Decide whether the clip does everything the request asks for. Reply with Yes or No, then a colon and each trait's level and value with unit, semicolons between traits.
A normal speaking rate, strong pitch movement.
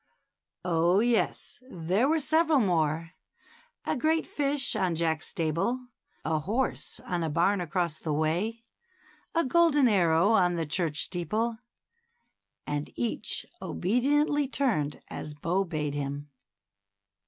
No: slow, 130 wpm; wide, 7.9 semitones